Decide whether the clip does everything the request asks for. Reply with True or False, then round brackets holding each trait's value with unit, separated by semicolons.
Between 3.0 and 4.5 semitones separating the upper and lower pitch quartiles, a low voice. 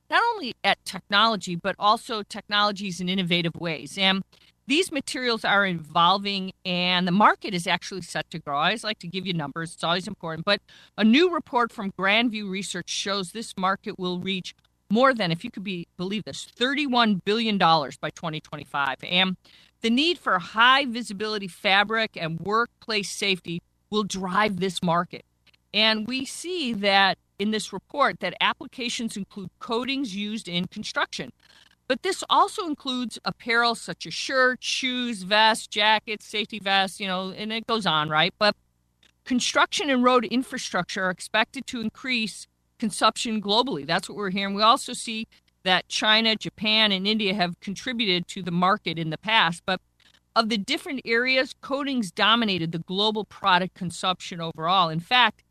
False (4.1 semitones; 205 Hz)